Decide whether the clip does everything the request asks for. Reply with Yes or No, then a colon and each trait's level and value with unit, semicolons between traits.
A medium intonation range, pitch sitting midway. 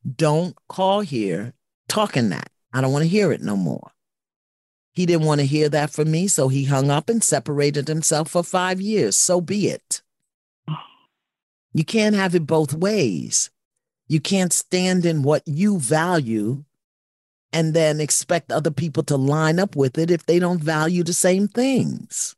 Yes: average, 3.8 semitones; medium, 160 Hz